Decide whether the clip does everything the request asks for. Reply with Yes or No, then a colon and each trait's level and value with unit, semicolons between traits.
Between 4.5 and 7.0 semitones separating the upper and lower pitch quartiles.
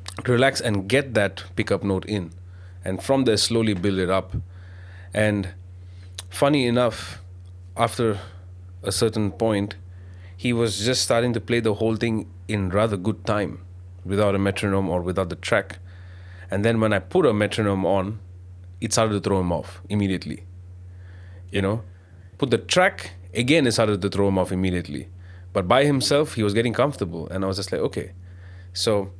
No: average, 3.3 semitones